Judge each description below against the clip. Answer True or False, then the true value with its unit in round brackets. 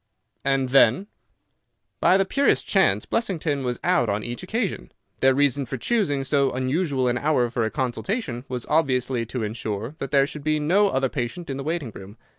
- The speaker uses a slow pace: False (185 wpm)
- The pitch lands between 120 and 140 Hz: True (135 Hz)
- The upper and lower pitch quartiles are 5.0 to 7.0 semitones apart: False (4.3 semitones)